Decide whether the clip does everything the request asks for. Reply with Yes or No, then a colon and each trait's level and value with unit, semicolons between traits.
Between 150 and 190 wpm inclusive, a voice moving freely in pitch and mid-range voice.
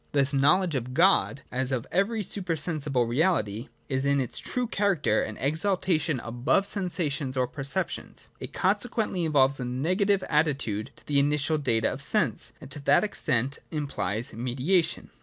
Yes: average, 155 wpm; wide, 5.7 semitones; medium, 145 Hz